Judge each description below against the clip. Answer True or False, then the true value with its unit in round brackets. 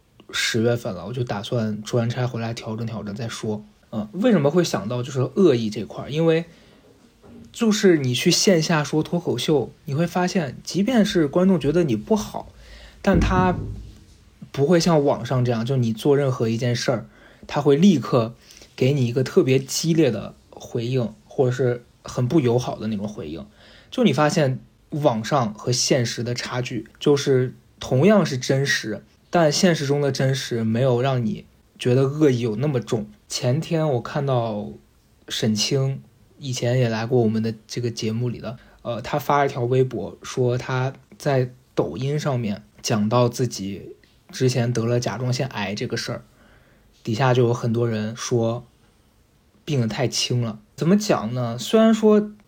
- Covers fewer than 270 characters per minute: True (245 characters per minute)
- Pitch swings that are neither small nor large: True (4.4 semitones)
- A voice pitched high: False (125 Hz)